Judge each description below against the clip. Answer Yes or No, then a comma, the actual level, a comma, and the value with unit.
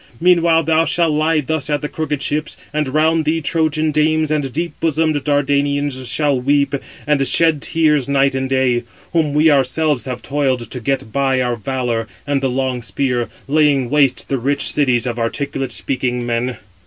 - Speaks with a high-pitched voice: No, medium, 140 Hz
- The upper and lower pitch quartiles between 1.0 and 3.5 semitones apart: Yes, average, 2.9 semitones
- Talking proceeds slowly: No, average, 175 wpm